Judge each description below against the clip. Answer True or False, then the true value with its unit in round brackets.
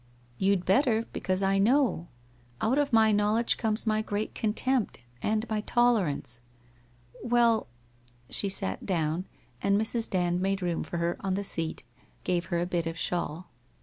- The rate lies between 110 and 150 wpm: False (165 wpm)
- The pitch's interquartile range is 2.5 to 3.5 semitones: False (4.2 semitones)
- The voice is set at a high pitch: True (195 Hz)